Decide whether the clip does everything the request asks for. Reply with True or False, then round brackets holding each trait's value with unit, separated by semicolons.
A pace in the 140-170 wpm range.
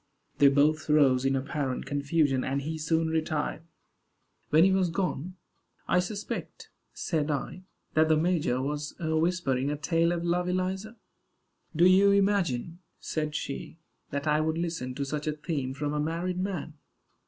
True (155 wpm)